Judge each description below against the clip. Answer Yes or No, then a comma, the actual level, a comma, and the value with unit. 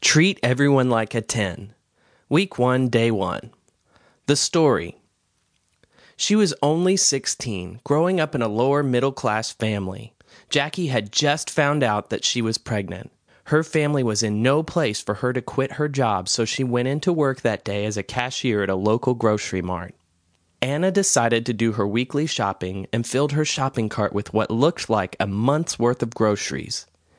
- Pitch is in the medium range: No, low, 120 Hz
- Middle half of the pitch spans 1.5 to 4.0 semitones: No, average, 5.3 semitones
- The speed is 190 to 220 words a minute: No, average, 175 wpm